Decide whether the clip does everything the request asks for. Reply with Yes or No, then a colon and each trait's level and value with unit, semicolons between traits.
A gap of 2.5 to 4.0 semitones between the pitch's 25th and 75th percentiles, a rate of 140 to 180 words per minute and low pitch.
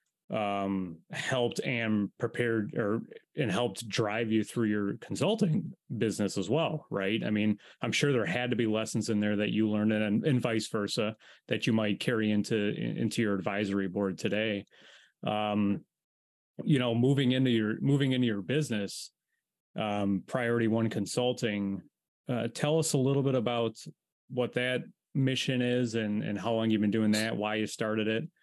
Yes: average, 3.2 semitones; average, 170 wpm; low, 110 Hz